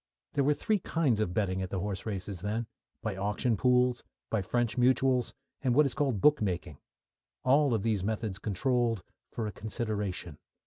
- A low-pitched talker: Yes, low, 110 Hz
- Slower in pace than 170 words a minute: No, average, 175 wpm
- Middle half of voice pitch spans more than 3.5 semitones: Yes, average, 4.0 semitones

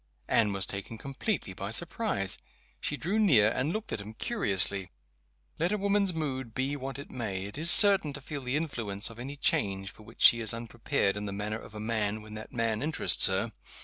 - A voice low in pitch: Yes, low, 115 Hz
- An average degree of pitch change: No, wide, 6.1 semitones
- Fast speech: Yes, fast, 210 wpm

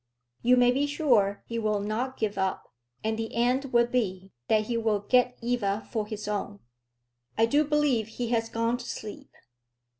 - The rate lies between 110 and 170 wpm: No, average, 180 wpm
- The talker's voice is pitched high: Yes, high, 230 Hz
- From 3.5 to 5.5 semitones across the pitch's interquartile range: No, average, 2.8 semitones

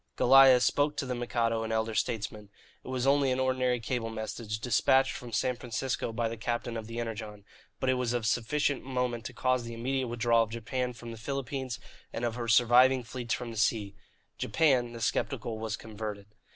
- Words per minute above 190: Yes, average, 200 wpm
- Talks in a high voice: No, low, 120 Hz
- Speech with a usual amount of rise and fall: No, narrow, 2.3 semitones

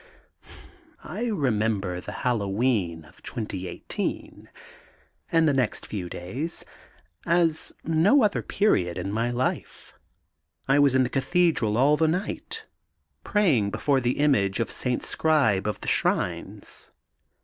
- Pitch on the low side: Yes, low, 130 Hz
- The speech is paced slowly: Yes, slow, 125 wpm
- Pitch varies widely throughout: Yes, wide, 7.4 semitones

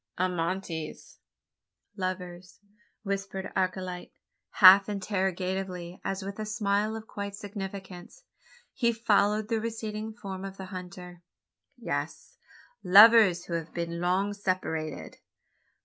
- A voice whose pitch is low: No, high, 190 Hz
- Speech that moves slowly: Yes, slow, 105 wpm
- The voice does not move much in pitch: Yes, narrow, 2.3 semitones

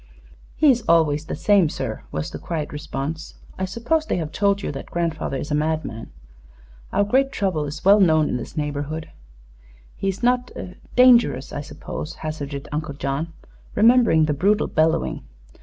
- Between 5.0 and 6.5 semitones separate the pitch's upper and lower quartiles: Yes, wide, 5.4 semitones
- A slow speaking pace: No, average, 165 wpm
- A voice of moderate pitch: Yes, medium, 160 Hz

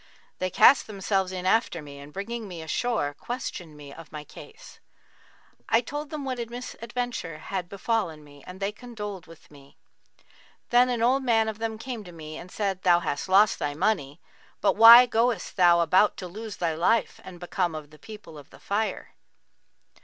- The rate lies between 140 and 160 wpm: No, average, 185 wpm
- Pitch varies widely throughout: Yes, wide, 5.7 semitones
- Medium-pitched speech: No, high, 195 Hz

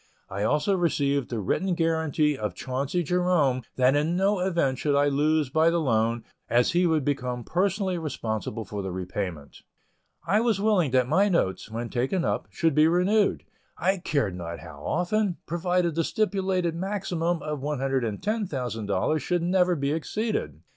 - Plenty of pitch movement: Yes, wide, 6.2 semitones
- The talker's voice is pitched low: No, medium, 155 Hz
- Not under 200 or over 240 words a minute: No, average, 160 wpm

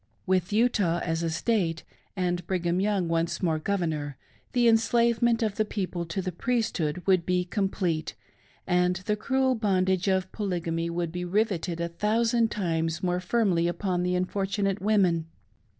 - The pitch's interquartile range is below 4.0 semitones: Yes, average, 3.6 semitones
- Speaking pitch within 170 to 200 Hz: Yes, medium, 185 Hz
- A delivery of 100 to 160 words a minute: Yes, average, 150 wpm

